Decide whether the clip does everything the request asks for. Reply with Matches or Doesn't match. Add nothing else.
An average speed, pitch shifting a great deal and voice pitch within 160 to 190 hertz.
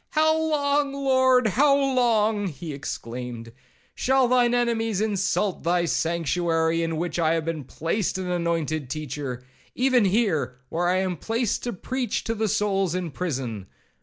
Matches